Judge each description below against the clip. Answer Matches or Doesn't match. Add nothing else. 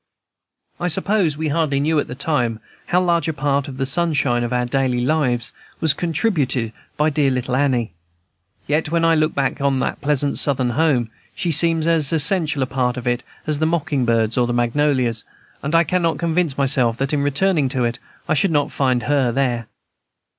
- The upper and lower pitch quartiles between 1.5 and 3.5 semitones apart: Doesn't match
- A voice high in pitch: Doesn't match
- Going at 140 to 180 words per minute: Doesn't match